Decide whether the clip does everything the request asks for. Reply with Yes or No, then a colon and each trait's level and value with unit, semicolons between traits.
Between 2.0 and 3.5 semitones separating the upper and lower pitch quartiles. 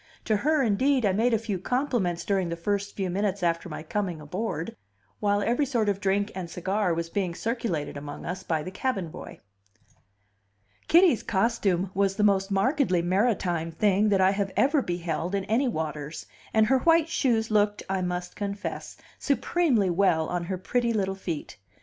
No: average, 4.2 semitones